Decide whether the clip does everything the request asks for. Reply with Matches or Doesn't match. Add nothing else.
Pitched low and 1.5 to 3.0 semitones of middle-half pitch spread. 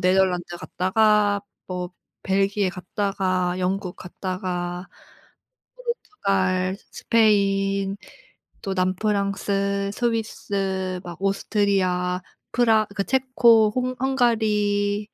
Doesn't match